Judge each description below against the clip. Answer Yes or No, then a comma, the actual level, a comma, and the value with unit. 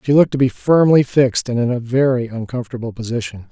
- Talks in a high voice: No, low, 125 Hz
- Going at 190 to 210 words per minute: Yes, fast, 205 wpm